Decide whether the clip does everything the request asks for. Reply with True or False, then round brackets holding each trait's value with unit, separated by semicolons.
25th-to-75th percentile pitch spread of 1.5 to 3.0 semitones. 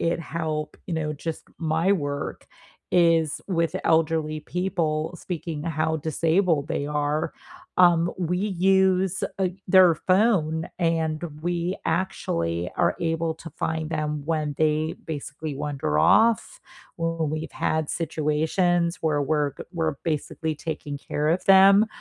True (2.4 semitones)